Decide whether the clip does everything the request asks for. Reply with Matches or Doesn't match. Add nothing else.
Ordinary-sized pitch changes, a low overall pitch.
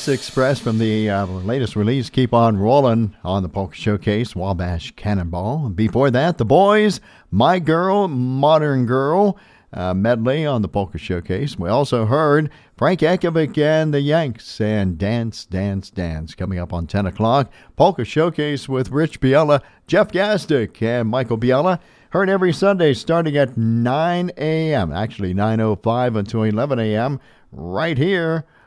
Doesn't match